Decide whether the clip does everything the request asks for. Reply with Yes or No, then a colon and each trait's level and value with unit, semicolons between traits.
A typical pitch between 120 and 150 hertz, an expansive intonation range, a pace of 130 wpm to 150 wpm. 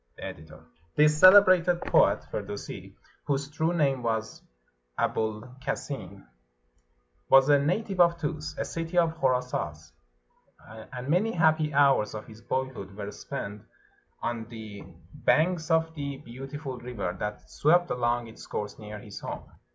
Yes: low, 135 Hz; wide, 6.4 semitones; slow, 135 wpm